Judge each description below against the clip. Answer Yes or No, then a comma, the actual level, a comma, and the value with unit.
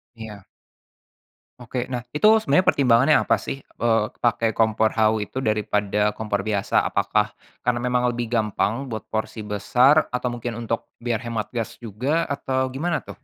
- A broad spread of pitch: No, narrow, 2.6 semitones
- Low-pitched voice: Yes, low, 115 Hz